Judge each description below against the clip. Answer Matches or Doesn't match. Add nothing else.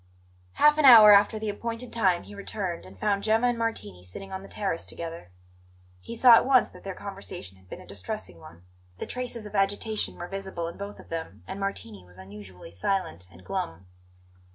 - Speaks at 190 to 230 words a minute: Matches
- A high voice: Matches